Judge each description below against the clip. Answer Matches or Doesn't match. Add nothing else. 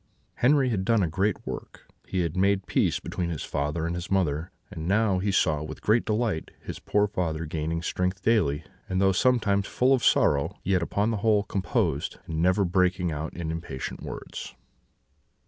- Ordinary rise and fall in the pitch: Matches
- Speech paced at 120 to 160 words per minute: Doesn't match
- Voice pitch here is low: Matches